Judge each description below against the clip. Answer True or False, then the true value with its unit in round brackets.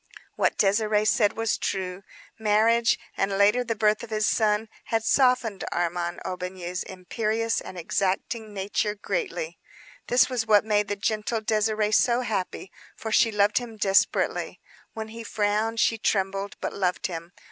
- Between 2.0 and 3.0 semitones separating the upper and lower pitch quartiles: True (2.5 semitones)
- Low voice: False (210 Hz)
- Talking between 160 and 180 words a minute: False (150 wpm)